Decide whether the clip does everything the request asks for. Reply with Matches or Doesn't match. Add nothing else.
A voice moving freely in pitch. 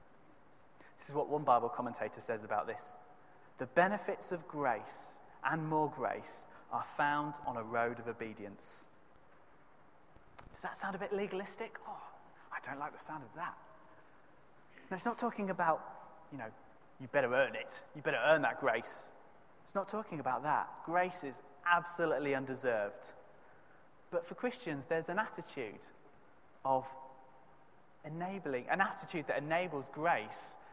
Matches